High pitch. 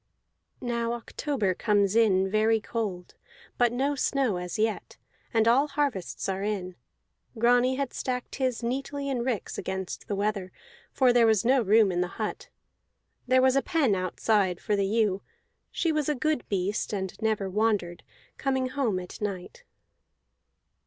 Yes: high, 225 Hz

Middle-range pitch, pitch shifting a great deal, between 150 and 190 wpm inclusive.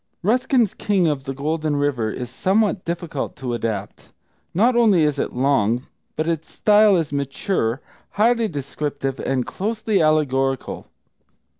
No: medium, 155 Hz; wide, 7.0 semitones; slow, 135 wpm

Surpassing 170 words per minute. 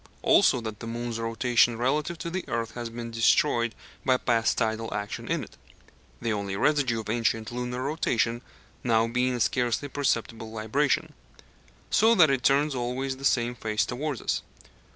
No: average, 165 wpm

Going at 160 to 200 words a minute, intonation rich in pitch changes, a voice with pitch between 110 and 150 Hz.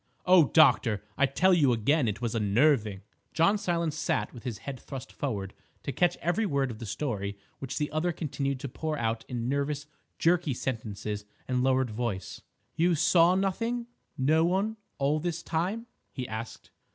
Yes: average, 165 wpm; wide, 6.2 semitones; medium, 140 Hz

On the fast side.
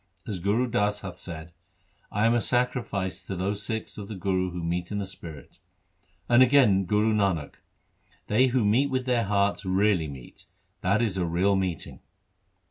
No: average, 185 wpm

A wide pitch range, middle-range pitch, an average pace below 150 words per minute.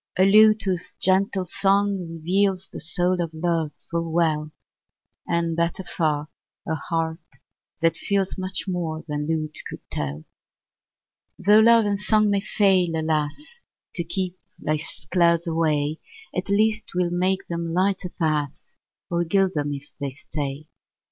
No: average, 3.4 semitones; medium, 170 Hz; average, 140 wpm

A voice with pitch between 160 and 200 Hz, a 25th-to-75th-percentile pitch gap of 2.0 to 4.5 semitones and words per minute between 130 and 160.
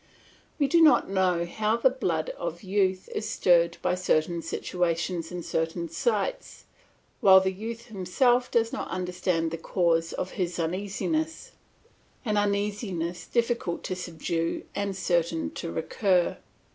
Yes: medium, 185 Hz; average, 3.9 semitones; slow, 135 wpm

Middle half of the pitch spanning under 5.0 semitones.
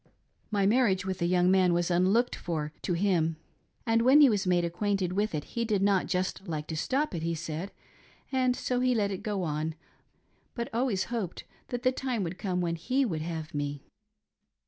No: average, 5.3 semitones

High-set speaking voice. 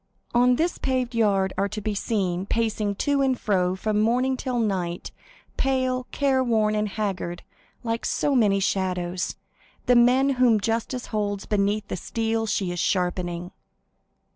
Yes: high, 215 Hz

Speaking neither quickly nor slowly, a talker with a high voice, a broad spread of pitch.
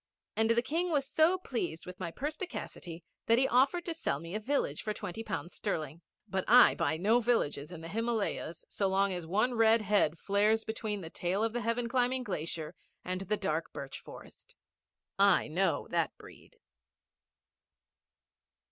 Yes: average, 170 wpm; high, 210 Hz; wide, 5.7 semitones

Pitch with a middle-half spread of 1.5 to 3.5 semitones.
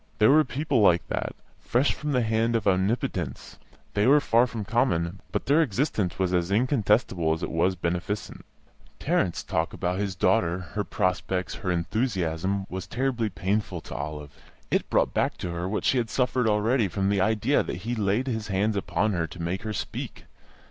No: average, 4.4 semitones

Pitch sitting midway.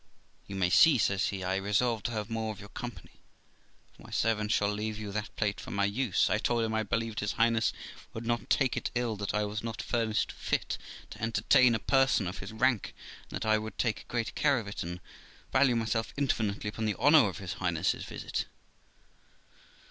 No: low, 110 Hz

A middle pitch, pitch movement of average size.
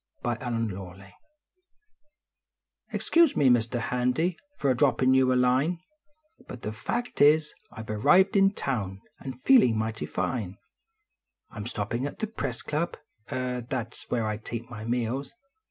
No: low, 125 Hz; average, 3.8 semitones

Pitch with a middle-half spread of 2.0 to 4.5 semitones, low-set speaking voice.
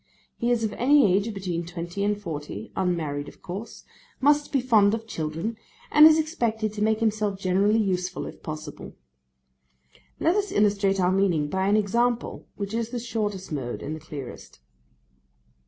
No: average, 4.1 semitones; high, 205 Hz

